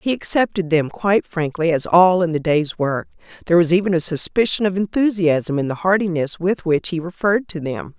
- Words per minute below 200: No, fast, 205 wpm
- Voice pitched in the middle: Yes, medium, 175 Hz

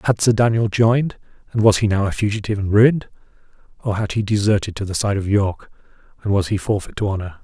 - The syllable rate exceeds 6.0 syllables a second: Yes, 6.6 syllables/s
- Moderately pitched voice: No, low, 105 Hz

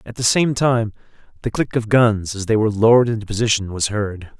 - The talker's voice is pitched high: No, low, 110 Hz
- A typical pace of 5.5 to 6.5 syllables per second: Yes, 5.9 syllables/s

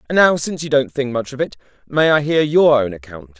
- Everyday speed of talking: No, fast, 265 wpm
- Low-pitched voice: Yes, low, 130 Hz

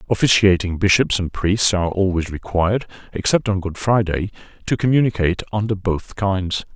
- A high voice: No, very low, 95 Hz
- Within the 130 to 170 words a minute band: Yes, average, 140 wpm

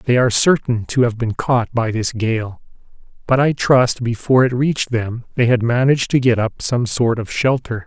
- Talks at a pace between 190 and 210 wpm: Yes, fast, 205 wpm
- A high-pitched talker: No, low, 120 Hz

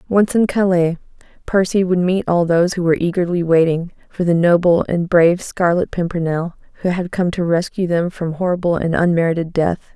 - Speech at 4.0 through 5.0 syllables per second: No, 5.5 syllables/s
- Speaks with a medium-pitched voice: Yes, medium, 175 Hz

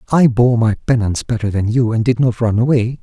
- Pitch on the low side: Yes, low, 115 Hz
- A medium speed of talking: No, fast, 240 wpm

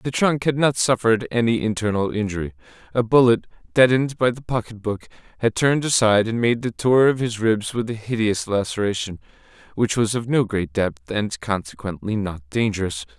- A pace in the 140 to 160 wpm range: No, average, 175 wpm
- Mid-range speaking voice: No, low, 115 Hz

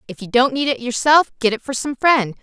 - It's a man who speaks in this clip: No, female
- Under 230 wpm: No, fast, 270 wpm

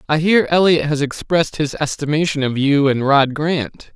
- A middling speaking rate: Yes, average, 180 wpm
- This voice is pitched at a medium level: Yes, medium, 150 Hz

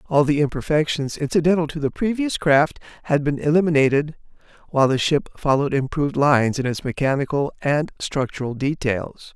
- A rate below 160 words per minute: Yes, average, 150 wpm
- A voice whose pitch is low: No, medium, 145 Hz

